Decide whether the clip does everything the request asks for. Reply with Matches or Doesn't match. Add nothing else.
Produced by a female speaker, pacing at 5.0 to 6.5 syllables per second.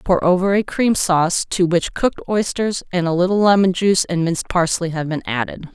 Matches